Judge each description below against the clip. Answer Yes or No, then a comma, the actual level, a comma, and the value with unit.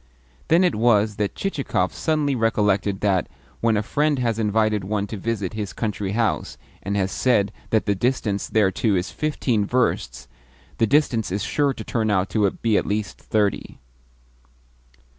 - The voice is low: Yes, low, 110 Hz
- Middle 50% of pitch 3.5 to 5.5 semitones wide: No, average, 2.8 semitones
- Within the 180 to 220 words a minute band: No, average, 160 wpm